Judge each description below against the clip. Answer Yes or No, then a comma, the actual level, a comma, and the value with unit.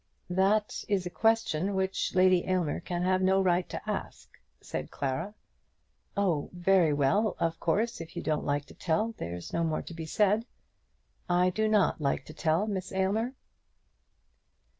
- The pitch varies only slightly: No, average, 3.7 semitones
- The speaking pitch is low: No, medium, 185 Hz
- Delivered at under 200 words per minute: Yes, average, 160 wpm